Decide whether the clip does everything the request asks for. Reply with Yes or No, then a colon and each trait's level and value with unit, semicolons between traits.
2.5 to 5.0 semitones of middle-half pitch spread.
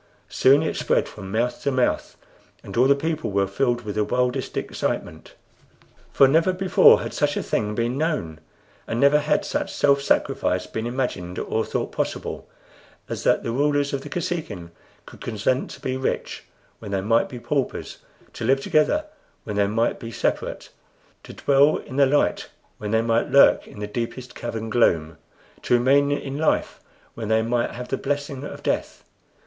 Yes: average, 4.3 semitones